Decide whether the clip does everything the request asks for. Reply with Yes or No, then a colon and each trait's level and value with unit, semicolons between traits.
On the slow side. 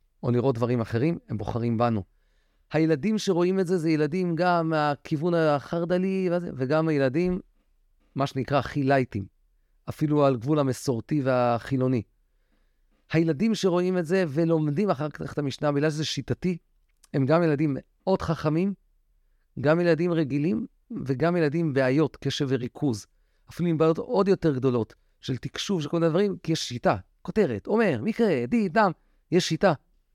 No: average, 145 wpm